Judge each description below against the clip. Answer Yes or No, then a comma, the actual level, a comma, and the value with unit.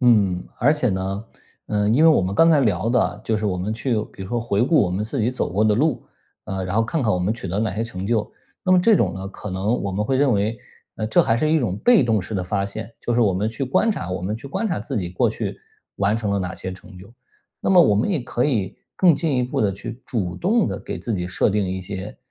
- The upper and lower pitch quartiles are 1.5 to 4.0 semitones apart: No, average, 4.6 semitones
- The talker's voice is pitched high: No, low, 110 Hz